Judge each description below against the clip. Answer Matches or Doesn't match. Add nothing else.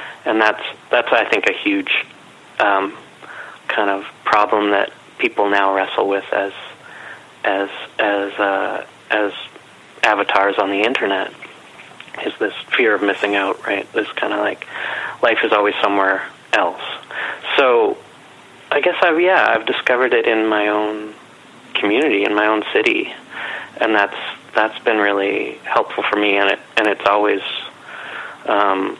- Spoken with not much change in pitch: Matches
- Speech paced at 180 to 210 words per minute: Doesn't match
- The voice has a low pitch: Matches